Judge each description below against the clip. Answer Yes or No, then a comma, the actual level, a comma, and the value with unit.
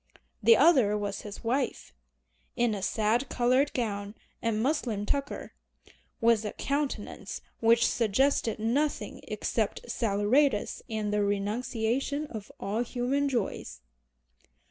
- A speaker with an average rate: No, slow, 115 wpm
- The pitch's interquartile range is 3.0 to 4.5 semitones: Yes, average, 4.2 semitones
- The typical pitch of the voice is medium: No, high, 230 Hz